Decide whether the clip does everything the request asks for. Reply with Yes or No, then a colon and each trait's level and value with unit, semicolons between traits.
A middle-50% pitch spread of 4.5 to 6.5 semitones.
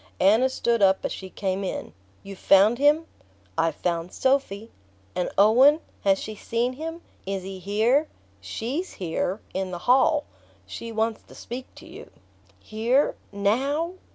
Yes: average, 5.3 semitones